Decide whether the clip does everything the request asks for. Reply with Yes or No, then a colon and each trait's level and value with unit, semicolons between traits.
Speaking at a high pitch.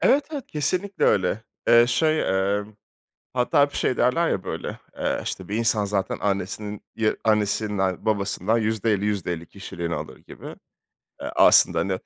No: low, 105 Hz